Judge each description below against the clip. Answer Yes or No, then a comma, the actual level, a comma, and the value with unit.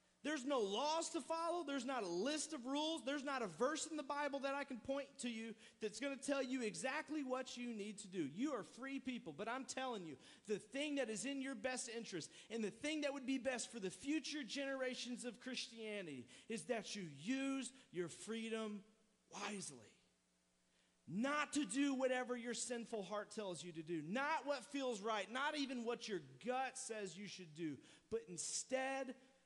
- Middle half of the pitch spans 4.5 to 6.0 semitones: Yes, average, 4.8 semitones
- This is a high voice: Yes, very high, 250 Hz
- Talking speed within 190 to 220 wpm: Yes, average, 200 wpm